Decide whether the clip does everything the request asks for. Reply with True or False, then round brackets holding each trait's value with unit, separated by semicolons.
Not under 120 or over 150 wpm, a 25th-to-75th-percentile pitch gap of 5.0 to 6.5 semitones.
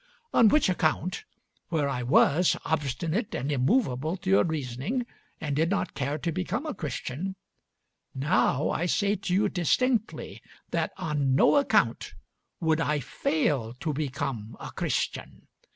True (140 wpm; 5.3 semitones)